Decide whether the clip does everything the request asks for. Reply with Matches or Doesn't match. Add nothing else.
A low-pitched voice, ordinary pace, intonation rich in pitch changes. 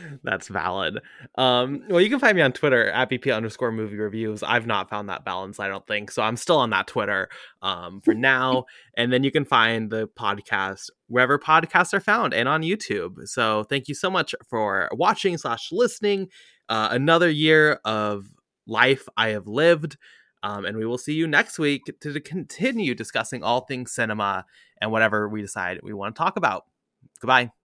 Matches